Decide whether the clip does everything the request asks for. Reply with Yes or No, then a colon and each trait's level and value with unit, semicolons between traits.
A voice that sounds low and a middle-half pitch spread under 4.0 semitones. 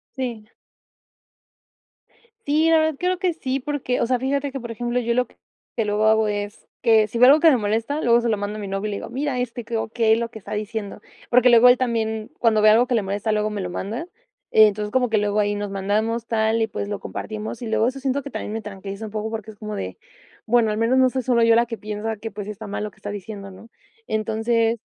No: high, 225 Hz; average, 2.8 semitones